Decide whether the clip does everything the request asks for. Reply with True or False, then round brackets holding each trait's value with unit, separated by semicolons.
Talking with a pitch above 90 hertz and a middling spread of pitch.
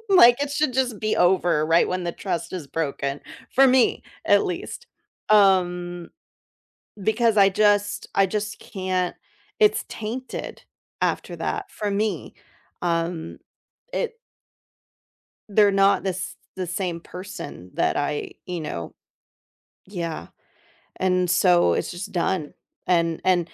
True (185 Hz; 3.5 semitones)